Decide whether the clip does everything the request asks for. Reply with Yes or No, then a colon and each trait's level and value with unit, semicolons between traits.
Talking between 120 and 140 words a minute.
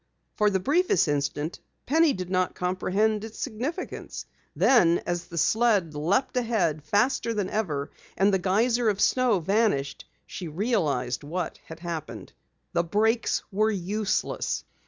Yes: slow, 135 wpm